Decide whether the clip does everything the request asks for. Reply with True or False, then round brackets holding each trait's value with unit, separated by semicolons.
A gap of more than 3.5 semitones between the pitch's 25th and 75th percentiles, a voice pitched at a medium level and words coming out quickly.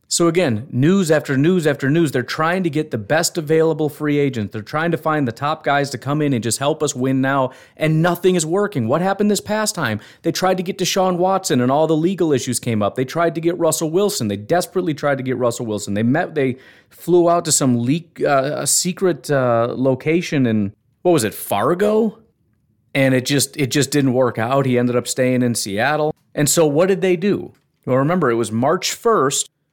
True (5.2 semitones; 150 Hz; 225 wpm)